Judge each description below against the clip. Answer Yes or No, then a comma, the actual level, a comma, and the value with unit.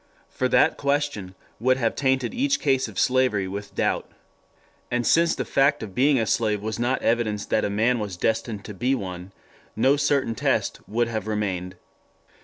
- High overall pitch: No, low, 115 Hz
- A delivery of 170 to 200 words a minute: Yes, average, 180 wpm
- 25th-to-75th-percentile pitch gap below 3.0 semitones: No, average, 4.2 semitones